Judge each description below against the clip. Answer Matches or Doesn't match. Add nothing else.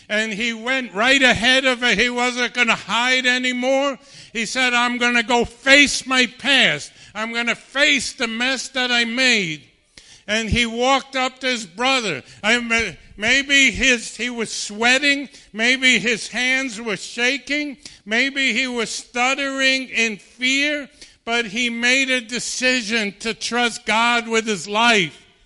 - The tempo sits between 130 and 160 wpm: Matches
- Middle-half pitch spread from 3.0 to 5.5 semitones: Doesn't match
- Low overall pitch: Doesn't match